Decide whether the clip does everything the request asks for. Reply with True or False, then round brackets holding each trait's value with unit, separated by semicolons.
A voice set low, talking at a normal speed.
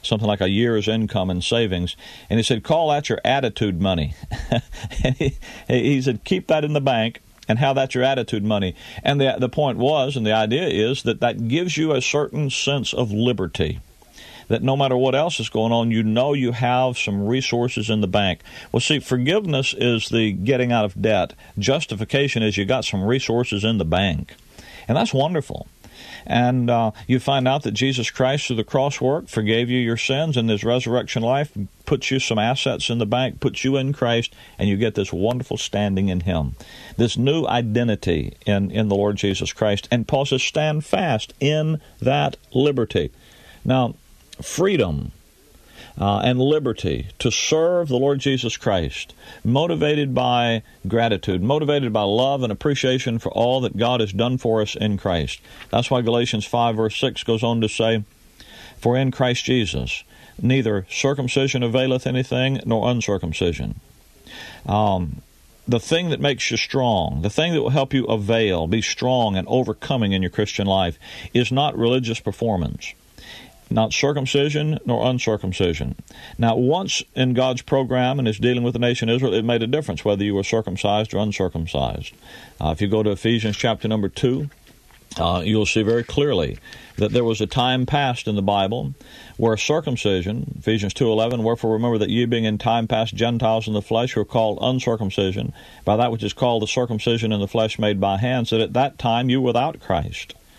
True (115 Hz; 185 wpm)